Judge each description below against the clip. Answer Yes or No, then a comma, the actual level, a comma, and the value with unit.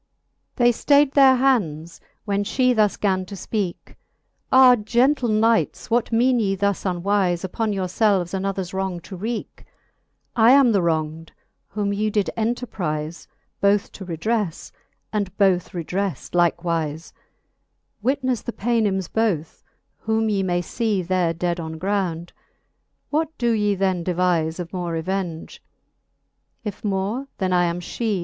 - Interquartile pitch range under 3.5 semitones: No, average, 4.2 semitones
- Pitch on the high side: Yes, high, 195 Hz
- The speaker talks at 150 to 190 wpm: No, average, 140 wpm